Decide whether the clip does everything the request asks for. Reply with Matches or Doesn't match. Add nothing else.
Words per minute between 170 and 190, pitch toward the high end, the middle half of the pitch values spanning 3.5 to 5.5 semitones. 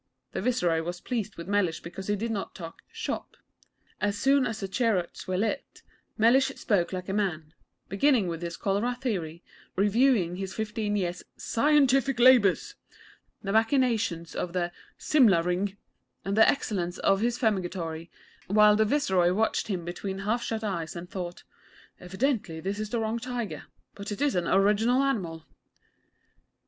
Doesn't match